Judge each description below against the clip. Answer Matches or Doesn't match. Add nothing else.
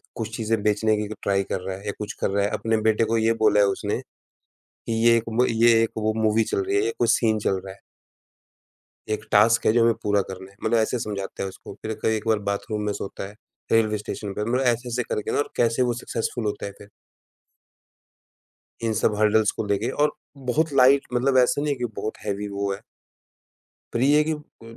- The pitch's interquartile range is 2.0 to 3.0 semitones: Matches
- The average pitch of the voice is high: Doesn't match